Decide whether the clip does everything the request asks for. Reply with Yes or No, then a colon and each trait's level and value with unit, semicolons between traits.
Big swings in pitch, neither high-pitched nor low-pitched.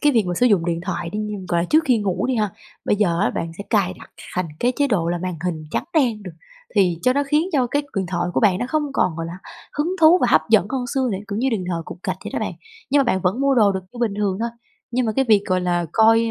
No: wide, 5.9 semitones; high, 210 Hz